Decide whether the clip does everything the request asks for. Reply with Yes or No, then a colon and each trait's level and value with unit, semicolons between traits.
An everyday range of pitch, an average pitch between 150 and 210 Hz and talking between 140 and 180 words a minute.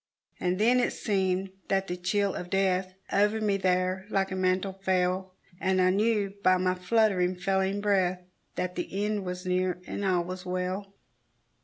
No: narrow, 1.4 semitones; high, 190 Hz; average, 170 wpm